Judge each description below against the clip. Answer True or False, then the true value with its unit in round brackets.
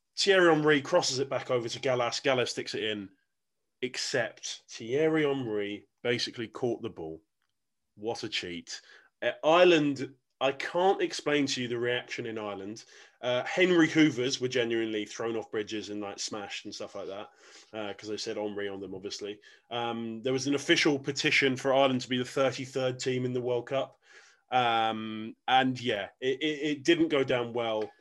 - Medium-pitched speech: False (125 Hz)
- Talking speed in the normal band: True (180 wpm)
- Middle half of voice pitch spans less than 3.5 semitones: False (4.0 semitones)